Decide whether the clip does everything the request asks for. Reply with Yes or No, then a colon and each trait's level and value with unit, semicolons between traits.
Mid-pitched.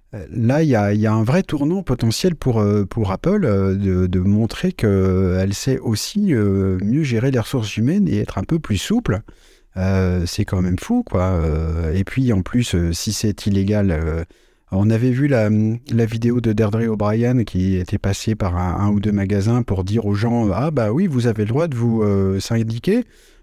No: low, 105 Hz